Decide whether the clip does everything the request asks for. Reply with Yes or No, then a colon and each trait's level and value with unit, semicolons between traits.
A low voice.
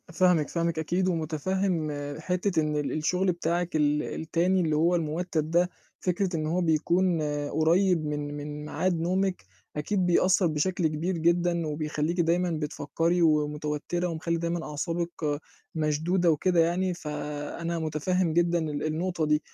No: medium, 165 Hz